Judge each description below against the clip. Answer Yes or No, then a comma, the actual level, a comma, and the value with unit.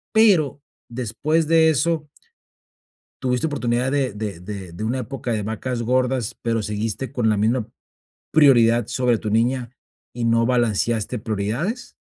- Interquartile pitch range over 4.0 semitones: No, average, 3.2 semitones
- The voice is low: Yes, low, 120 Hz